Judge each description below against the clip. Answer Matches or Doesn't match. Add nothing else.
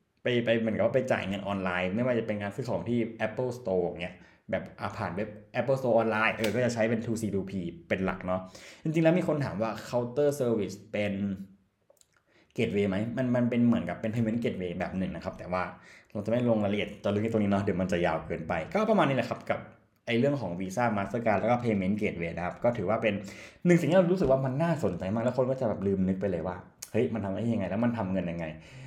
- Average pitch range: Matches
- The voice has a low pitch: Matches